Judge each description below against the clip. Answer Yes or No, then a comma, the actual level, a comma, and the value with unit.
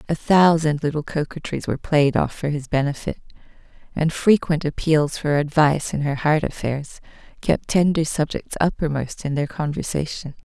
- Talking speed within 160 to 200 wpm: No, average, 150 wpm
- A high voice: No, medium, 150 Hz